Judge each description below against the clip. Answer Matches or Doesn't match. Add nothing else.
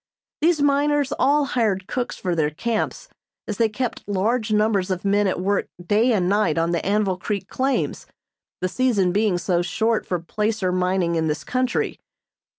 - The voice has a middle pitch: Doesn't match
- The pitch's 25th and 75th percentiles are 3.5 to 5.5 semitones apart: Matches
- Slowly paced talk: Doesn't match